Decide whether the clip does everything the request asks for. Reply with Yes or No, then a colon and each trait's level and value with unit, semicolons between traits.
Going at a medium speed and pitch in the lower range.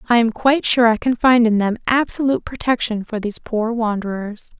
No: average, 195 wpm; high, 230 Hz